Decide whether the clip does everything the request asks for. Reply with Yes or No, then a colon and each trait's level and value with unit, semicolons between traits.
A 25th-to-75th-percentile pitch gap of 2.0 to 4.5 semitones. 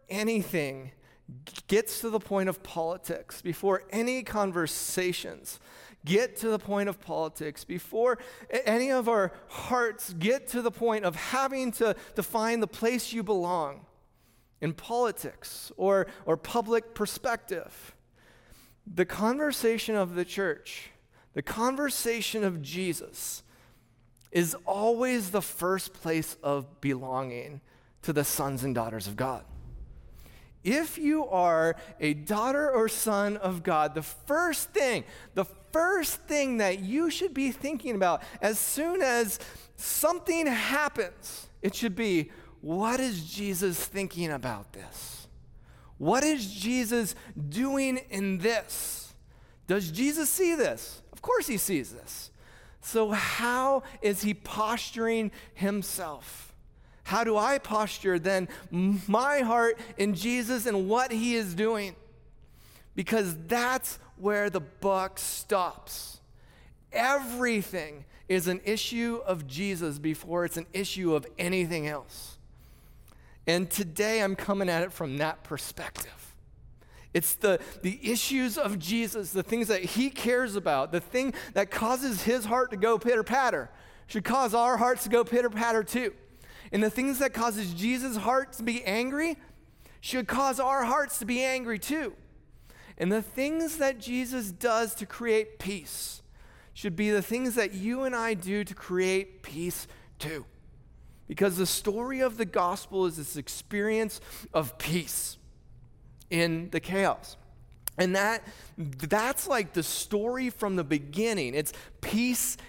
No: wide, 5.5 semitones